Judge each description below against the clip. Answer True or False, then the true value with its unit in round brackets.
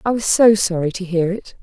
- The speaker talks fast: True (260 wpm)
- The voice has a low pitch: False (195 Hz)